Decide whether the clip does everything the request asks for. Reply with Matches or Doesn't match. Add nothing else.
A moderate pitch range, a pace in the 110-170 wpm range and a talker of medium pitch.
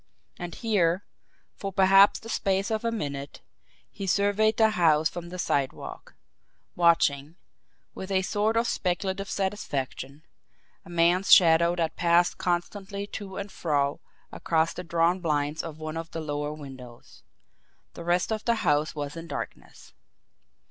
Matches